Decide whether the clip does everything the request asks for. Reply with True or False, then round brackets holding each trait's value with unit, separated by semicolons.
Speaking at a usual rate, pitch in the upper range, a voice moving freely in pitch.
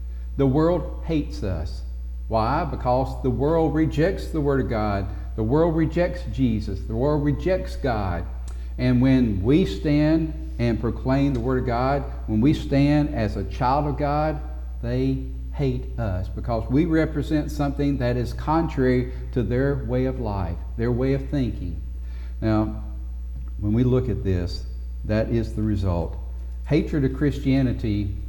False (150 wpm; 120 Hz; 7.0 semitones)